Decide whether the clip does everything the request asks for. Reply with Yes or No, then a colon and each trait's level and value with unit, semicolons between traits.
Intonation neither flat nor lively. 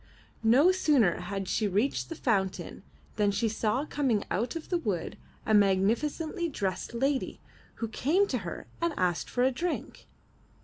No: wide, 6.7 semitones